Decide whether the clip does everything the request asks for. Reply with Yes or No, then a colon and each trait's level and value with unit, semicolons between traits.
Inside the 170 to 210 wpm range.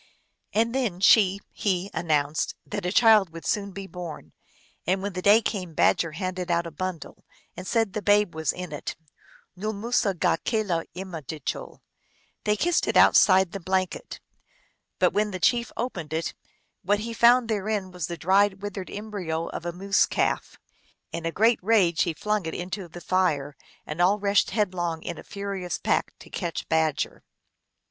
Yes: average, 175 wpm